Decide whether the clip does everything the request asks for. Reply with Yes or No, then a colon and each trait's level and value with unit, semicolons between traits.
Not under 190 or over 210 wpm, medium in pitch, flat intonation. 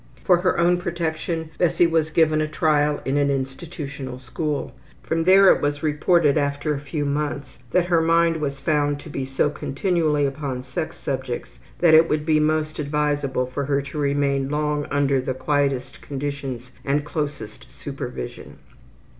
No: average, 165 wpm; medium, 145 Hz; narrow, 2.2 semitones